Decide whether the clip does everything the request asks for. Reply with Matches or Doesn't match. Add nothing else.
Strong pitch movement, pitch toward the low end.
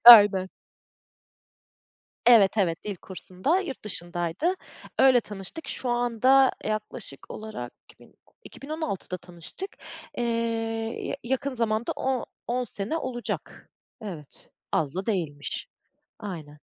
Doesn't match